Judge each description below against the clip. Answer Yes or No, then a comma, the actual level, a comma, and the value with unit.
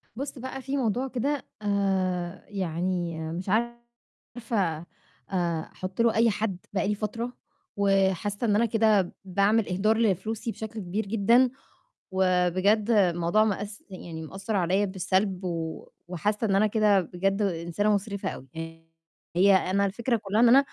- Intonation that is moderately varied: Yes, average, 3.2 semitones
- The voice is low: No, high, 200 Hz